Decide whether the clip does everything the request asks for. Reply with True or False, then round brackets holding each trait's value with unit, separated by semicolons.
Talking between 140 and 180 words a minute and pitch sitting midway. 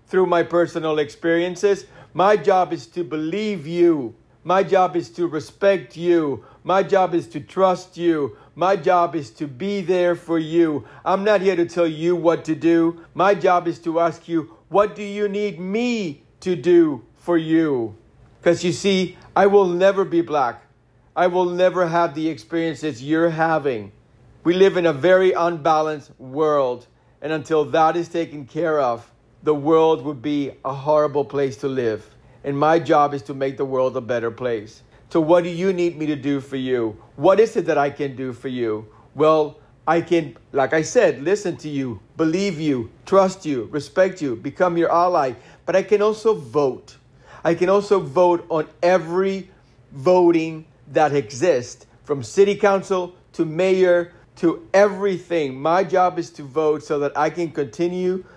True (175 wpm; 165 Hz)